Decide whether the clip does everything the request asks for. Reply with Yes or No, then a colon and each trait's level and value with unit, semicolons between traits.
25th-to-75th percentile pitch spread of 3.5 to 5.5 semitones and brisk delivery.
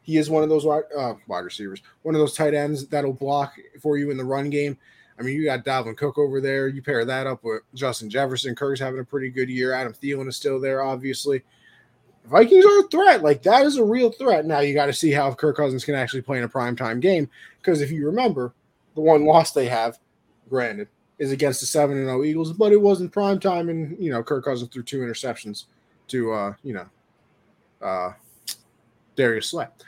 No: average, 3.0 semitones; fast, 220 wpm